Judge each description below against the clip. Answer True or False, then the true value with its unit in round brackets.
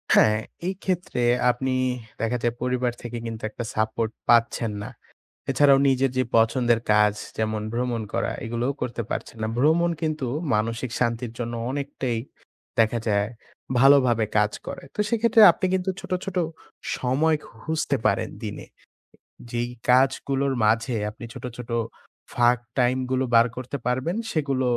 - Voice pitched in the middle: False (125 Hz)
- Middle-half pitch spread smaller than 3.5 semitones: True (3.0 semitones)